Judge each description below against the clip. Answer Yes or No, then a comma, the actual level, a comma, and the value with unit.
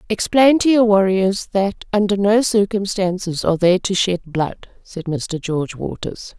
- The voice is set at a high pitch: Yes, high, 195 Hz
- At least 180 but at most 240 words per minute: No, average, 160 wpm